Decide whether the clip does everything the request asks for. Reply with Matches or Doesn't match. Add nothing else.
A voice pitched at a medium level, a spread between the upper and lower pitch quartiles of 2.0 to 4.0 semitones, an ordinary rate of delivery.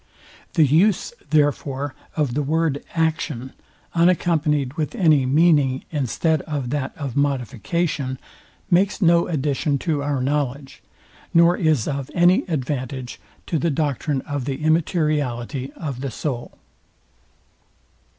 Doesn't match